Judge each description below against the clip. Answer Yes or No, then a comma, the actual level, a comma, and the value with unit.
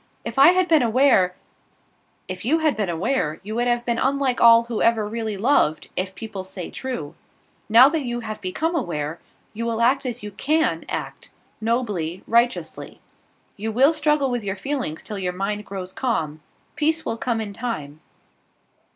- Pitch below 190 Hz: No, high, 230 Hz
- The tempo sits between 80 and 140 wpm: No, average, 175 wpm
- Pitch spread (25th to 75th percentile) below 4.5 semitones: No, average, 5.2 semitones